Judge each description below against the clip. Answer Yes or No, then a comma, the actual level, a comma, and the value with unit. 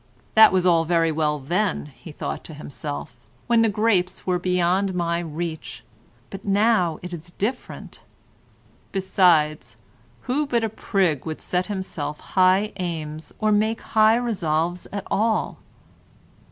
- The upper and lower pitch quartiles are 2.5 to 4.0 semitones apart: No, average, 4.4 semitones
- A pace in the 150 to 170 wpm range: No, average, 140 wpm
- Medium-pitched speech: Yes, medium, 180 Hz